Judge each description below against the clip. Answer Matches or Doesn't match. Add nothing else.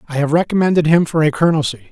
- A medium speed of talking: Doesn't match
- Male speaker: Matches